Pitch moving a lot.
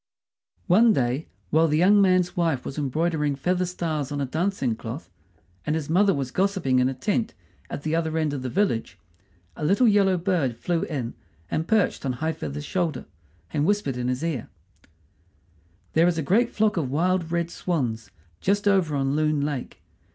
No: average, 4.8 semitones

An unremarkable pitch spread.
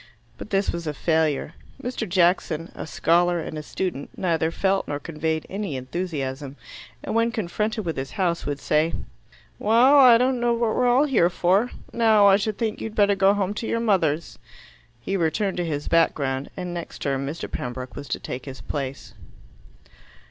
No: wide, 5.8 semitones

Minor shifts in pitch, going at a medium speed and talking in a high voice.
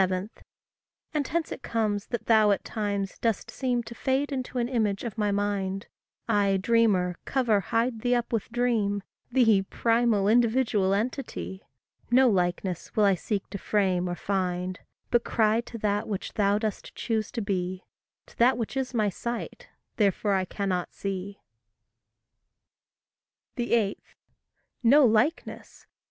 No: average, 3.3 semitones; average, 145 wpm; high, 215 Hz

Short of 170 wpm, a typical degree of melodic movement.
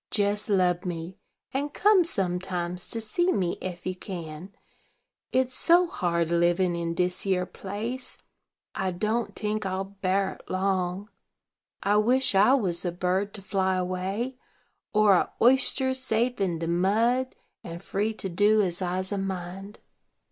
Yes: average, 150 wpm; average, 3.3 semitones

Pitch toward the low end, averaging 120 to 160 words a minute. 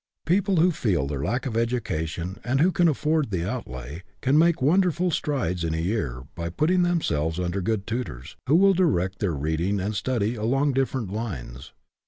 No: low, 110 Hz; average, 180 wpm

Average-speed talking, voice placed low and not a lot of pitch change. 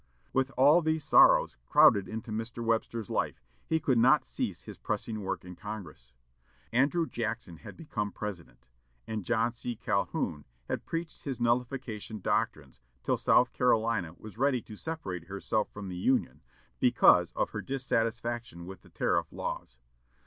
No: average, 150 wpm; low, 115 Hz; average, 4.1 semitones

